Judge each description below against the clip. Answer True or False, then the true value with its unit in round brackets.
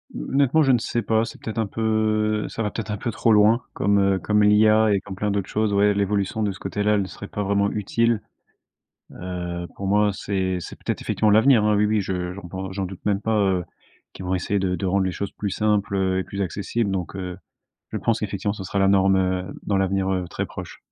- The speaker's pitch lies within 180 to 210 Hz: False (100 Hz)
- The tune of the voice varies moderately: False (2.0 semitones)